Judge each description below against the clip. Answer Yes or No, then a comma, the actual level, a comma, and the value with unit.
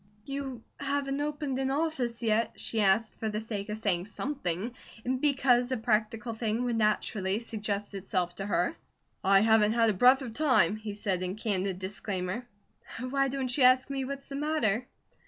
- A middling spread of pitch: Yes, average, 4.3 semitones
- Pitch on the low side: No, high, 225 Hz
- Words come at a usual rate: Yes, average, 175 wpm